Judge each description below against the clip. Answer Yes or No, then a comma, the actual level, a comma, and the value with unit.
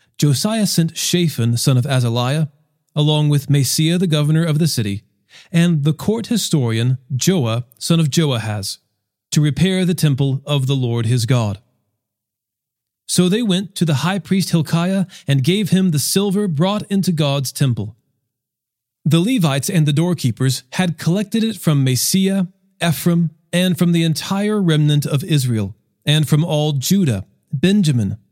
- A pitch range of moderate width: No, wide, 5.7 semitones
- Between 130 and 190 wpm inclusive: Yes, average, 150 wpm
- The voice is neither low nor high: Yes, medium, 155 Hz